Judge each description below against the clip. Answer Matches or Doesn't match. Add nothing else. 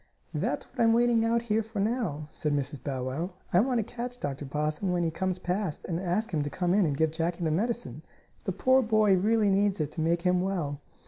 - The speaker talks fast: Matches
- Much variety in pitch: Matches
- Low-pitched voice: Doesn't match